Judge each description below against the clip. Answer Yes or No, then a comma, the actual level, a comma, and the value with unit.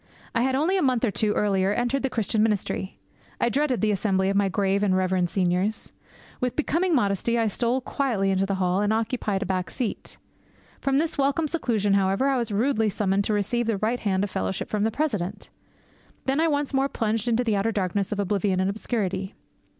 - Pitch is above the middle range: Yes, high, 215 Hz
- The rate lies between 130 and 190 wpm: No, fast, 205 wpm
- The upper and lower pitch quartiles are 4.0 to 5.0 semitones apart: Yes, average, 4.3 semitones